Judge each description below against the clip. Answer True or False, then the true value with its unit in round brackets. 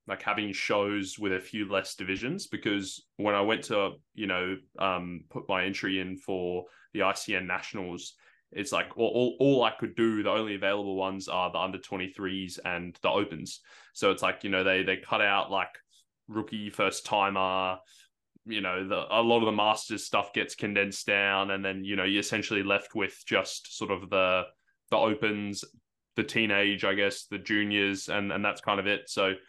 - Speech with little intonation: True (1.7 semitones)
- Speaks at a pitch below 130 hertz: True (100 Hz)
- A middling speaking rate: True (195 wpm)